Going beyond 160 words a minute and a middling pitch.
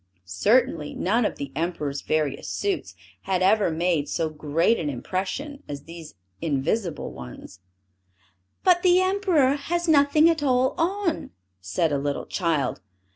No: slow, 135 wpm; medium, 180 Hz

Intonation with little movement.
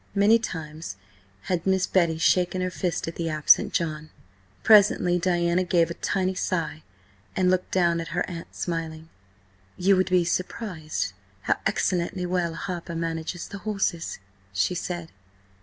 Yes: narrow, 2.0 semitones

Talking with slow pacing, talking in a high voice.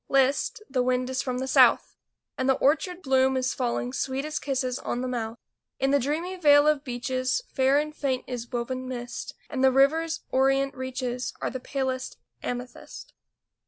No: average, 175 wpm; very high, 260 Hz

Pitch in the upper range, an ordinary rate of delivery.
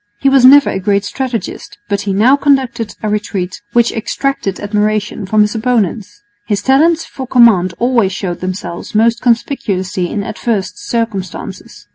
Yes: high, 215 Hz; average, 150 wpm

